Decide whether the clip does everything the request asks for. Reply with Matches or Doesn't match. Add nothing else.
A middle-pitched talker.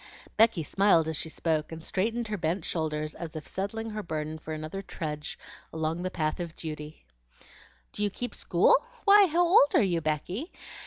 Matches